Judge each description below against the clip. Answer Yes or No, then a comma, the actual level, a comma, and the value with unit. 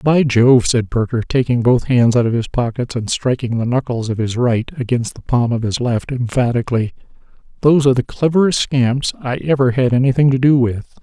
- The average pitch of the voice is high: No, low, 125 Hz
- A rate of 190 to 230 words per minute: Yes, average, 200 wpm